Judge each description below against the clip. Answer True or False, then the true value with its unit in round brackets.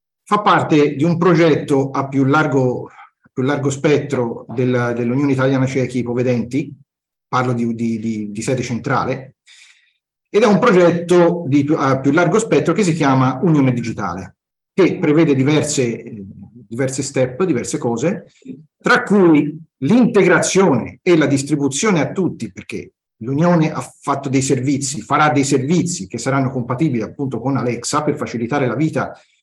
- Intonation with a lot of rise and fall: False (3.8 semitones)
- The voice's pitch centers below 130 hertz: False (140 Hz)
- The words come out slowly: False (135 wpm)